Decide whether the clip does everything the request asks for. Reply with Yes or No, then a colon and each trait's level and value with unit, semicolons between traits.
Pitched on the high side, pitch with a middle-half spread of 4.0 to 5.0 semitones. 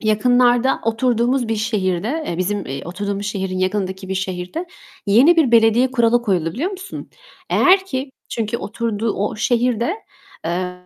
Yes: high, 225 Hz; average, 4.3 semitones